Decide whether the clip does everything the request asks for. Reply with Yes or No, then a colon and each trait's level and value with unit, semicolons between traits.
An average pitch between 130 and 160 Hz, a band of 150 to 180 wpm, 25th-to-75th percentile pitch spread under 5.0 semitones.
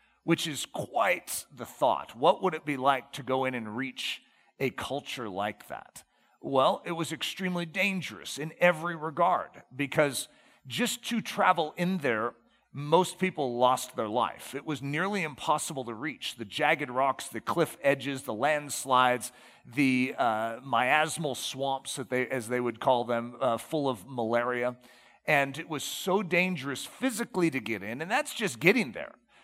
No: medium, 140 Hz; average, 165 wpm; average, 5.3 semitones